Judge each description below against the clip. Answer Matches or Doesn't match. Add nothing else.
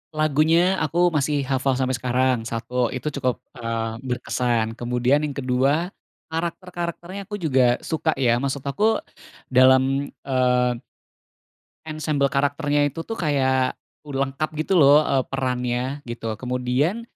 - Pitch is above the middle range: Doesn't match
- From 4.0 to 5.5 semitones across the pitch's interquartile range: Doesn't match